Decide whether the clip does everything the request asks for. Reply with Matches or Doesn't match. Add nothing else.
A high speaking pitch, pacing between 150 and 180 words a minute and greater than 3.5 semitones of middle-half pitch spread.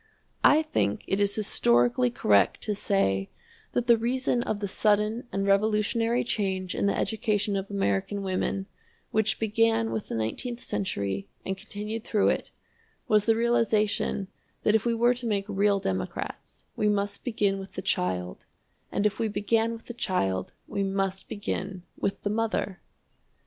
Doesn't match